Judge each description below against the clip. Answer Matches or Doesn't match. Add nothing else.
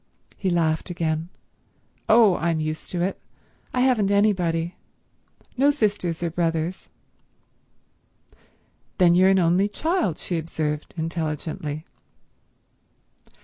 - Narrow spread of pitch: Doesn't match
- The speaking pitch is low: Doesn't match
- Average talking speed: Doesn't match